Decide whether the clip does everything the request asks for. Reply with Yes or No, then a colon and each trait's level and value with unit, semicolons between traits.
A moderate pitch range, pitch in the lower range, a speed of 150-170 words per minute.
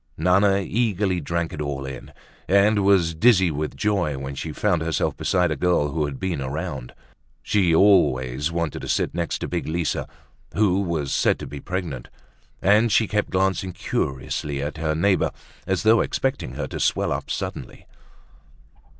Yes: average, 4.8 semitones; very low, 85 Hz; average, 165 wpm